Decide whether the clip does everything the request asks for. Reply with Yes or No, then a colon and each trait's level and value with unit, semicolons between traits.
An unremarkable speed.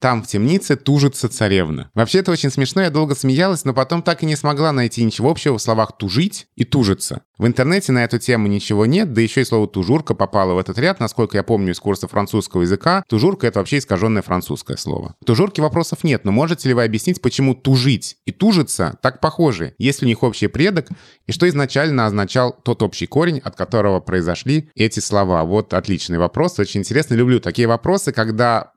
No: fast, 200 wpm